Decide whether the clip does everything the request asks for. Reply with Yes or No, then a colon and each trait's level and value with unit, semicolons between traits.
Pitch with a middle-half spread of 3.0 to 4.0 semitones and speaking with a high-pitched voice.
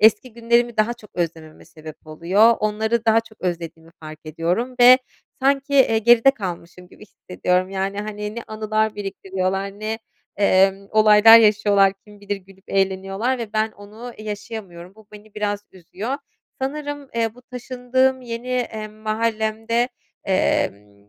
Yes: average, 3.3 semitones; high, 215 Hz